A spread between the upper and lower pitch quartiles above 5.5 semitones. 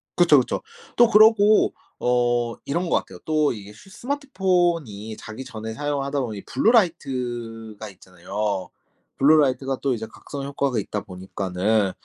Yes: wide, 6.5 semitones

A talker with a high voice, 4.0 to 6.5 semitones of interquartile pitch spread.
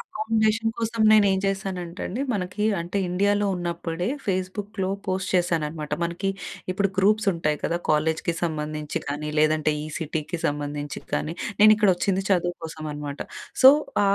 No: medium, 175 Hz; average, 4.5 semitones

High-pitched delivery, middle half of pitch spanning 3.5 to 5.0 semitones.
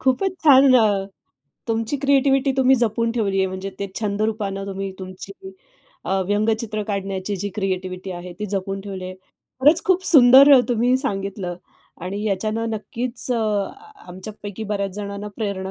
Yes: high, 205 Hz; average, 3.9 semitones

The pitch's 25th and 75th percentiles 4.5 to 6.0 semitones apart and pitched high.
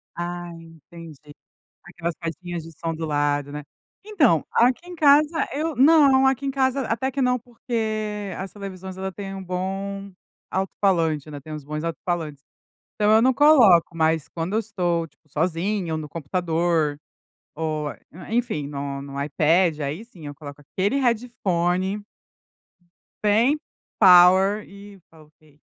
No: wide, 5.5 semitones; medium, 180 Hz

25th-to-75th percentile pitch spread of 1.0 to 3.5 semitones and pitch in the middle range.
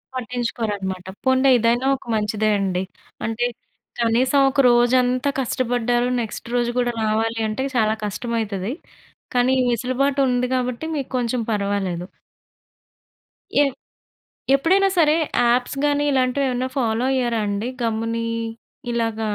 No: narrow, 2.6 semitones; high, 240 Hz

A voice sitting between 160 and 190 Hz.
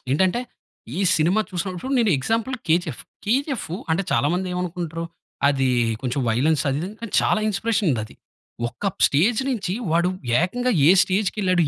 Yes: medium, 185 Hz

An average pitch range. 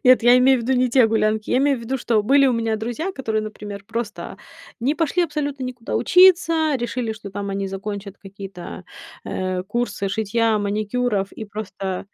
Yes: average, 4.1 semitones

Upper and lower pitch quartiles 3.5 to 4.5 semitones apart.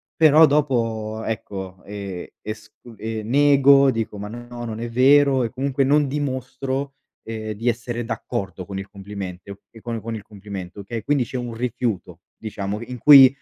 Yes: average, 4.2 semitones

